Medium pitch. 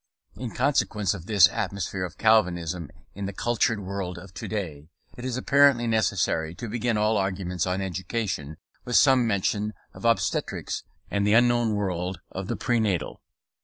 No: low, 100 Hz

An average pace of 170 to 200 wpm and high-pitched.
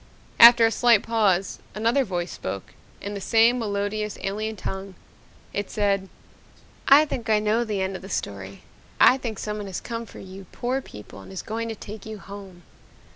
Yes: average, 180 wpm; high, 210 Hz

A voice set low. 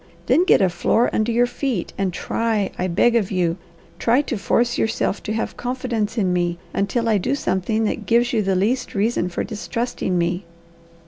No: high, 220 Hz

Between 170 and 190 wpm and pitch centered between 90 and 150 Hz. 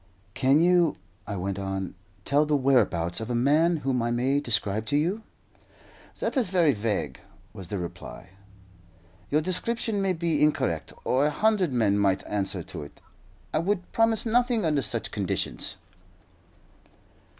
No: average, 150 wpm; medium, 140 Hz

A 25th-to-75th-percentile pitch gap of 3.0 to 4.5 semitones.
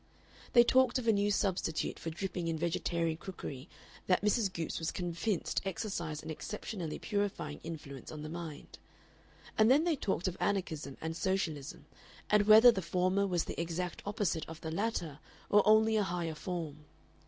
Yes: average, 4.2 semitones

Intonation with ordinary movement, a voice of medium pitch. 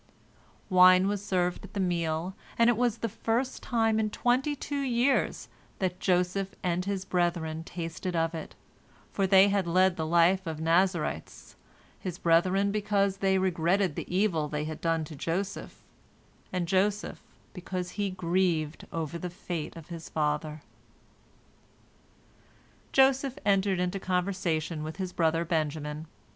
Yes: average, 3.2 semitones; medium, 180 Hz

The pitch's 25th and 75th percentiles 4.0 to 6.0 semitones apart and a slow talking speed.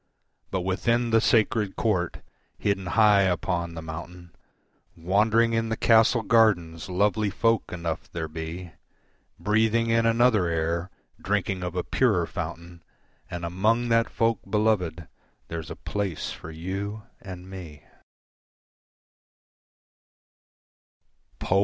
Yes: average, 4.6 semitones; slow, 115 wpm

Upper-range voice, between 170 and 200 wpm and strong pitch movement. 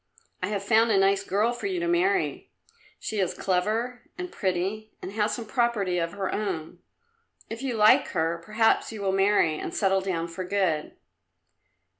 No: high, 200 Hz; average, 175 wpm; average, 3.4 semitones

